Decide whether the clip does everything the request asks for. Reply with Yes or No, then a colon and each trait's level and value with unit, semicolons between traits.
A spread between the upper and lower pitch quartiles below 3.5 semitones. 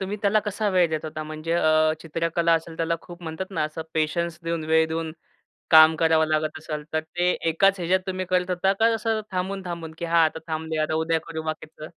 Yes: narrow, 2.5 semitones